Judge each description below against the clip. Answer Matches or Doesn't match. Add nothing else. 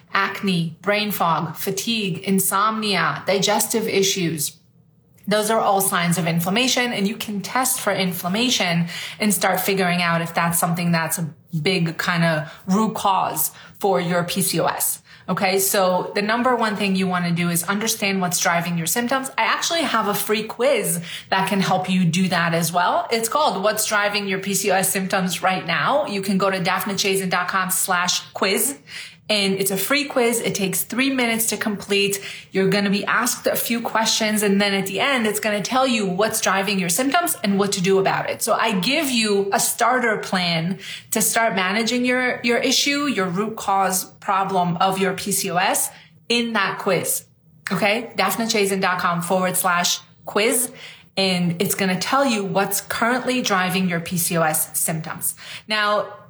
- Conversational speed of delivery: Matches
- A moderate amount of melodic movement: Matches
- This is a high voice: Matches